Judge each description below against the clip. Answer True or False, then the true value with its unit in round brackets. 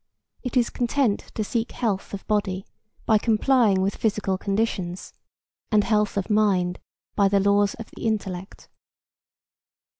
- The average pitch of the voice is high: True (205 Hz)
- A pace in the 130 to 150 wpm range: True (140 wpm)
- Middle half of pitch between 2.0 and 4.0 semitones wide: True (2.4 semitones)